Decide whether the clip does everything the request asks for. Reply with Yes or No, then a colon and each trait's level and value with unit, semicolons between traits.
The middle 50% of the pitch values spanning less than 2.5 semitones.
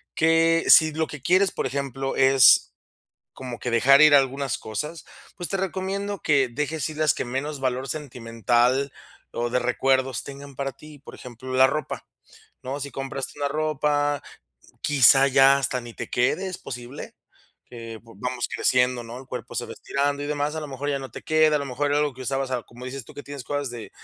No: average, 2.8 semitones